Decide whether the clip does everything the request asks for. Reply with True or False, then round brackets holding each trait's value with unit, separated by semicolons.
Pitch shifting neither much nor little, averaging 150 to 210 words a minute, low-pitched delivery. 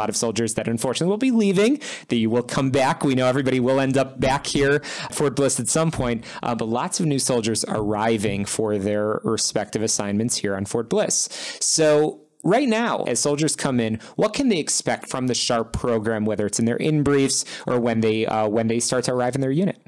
False (4.3 semitones; 225 wpm; 125 Hz)